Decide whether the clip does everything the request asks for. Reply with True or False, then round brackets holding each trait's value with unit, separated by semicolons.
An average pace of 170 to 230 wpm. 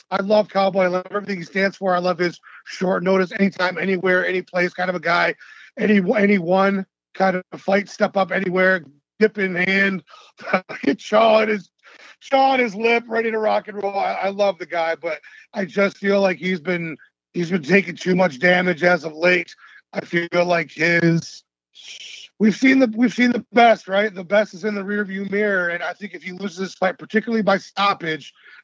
True (200 wpm)